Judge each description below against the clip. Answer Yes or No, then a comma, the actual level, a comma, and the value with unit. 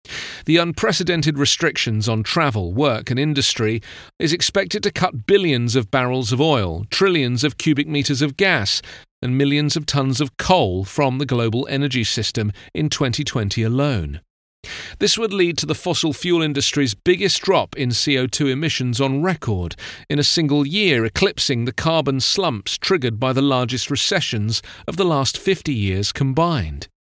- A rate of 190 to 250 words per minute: No, average, 155 wpm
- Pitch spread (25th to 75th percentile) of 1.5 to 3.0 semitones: No, average, 5.3 semitones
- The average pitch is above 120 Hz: Yes, medium, 140 Hz